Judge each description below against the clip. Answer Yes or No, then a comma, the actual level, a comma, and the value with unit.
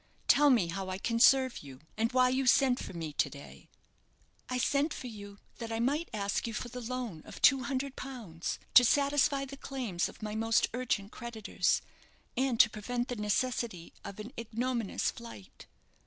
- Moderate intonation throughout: Yes, average, 3.7 semitones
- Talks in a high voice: Yes, high, 235 Hz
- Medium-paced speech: Yes, average, 185 wpm